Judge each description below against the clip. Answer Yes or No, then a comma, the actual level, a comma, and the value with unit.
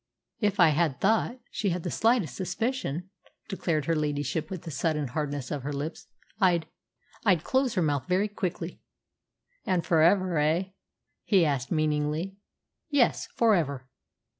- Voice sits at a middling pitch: Yes, medium, 170 Hz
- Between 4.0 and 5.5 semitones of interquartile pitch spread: Yes, average, 4.4 semitones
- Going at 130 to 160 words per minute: Yes, average, 145 wpm